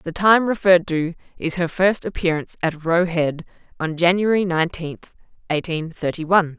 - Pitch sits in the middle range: Yes, medium, 170 Hz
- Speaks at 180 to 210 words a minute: No, average, 155 wpm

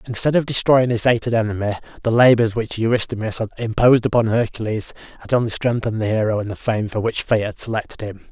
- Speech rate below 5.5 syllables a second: No, 6.3 syllables/s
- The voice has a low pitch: Yes, low, 115 Hz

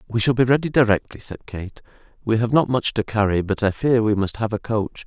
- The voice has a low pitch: Yes, low, 110 Hz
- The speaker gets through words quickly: Yes, fast, 250 wpm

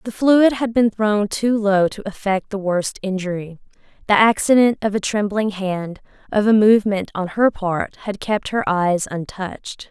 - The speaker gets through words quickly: No, average, 175 wpm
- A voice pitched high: Yes, high, 205 Hz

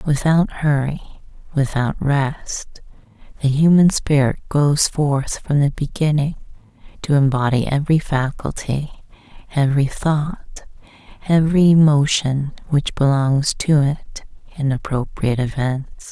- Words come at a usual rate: No, slow, 100 wpm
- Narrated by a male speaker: No, female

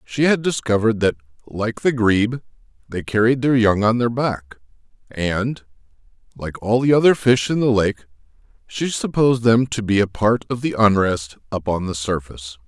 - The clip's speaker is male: Yes, male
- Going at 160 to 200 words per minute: Yes, average, 175 wpm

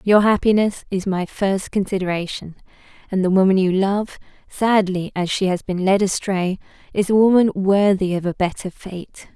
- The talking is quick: No, average, 165 wpm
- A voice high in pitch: Yes, high, 195 Hz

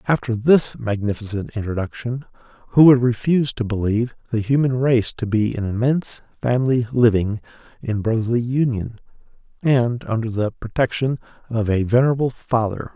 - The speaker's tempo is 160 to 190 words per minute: No, slow, 135 wpm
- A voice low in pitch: Yes, low, 120 Hz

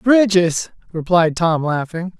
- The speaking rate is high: No, slow, 110 wpm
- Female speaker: No, male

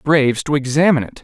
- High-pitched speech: No, medium, 140 Hz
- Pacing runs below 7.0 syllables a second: No, 7.2 syllables/s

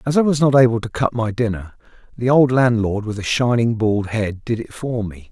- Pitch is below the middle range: Yes, low, 115 Hz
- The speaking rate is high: Yes, fast, 235 wpm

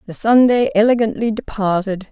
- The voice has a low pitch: No, high, 215 Hz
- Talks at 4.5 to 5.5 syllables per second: Yes, 5.3 syllables/s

